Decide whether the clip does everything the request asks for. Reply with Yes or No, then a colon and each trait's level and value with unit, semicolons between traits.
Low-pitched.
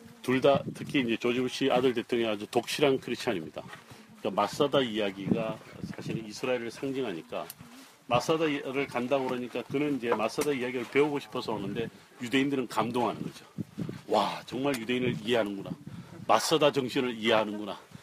Yes: low, 125 Hz